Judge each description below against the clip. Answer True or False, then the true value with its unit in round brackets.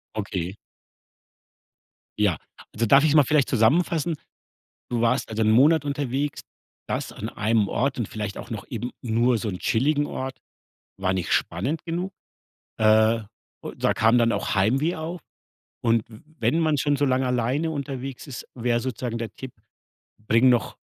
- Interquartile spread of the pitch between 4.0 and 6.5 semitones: True (4.5 semitones)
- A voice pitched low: True (125 Hz)